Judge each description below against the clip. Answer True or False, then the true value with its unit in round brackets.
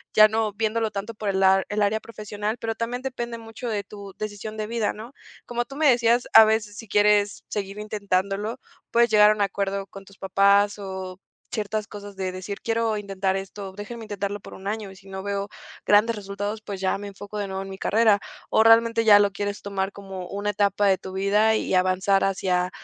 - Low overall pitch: False (205 Hz)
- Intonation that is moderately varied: False (1.9 semitones)